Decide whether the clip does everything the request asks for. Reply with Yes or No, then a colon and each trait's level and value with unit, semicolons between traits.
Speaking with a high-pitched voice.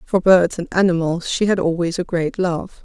No: medium, 175 Hz